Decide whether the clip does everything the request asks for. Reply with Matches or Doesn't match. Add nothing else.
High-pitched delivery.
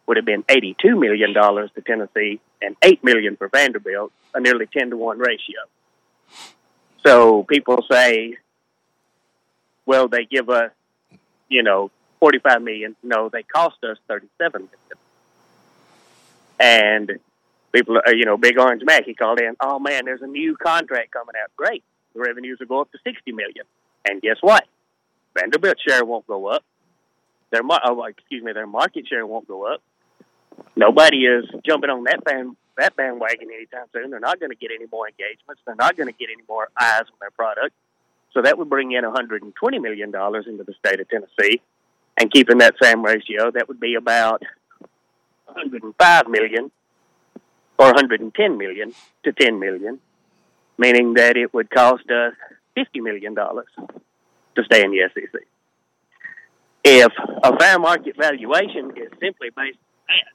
Doesn't match